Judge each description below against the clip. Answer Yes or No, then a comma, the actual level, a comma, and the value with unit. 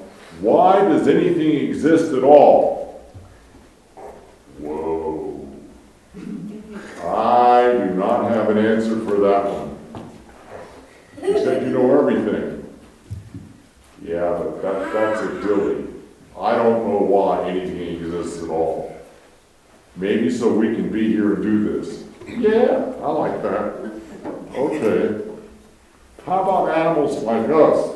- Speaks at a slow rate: Yes, slow, 115 wpm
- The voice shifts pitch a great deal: Yes, wide, 7.5 semitones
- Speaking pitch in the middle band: No, low, 110 Hz